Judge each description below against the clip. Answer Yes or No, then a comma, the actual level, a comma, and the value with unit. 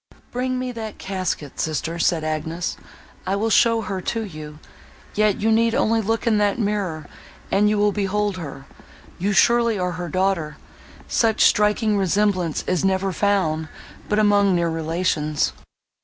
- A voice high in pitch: Yes, high, 195 Hz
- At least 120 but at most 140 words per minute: No, average, 155 wpm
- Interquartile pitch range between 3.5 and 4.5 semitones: Yes, average, 4.1 semitones